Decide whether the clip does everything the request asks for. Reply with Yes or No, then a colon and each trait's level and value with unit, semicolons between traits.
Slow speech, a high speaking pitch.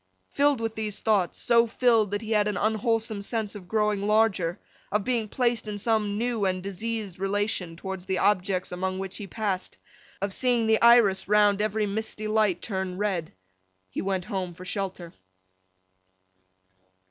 No: average, 155 wpm; high, 205 Hz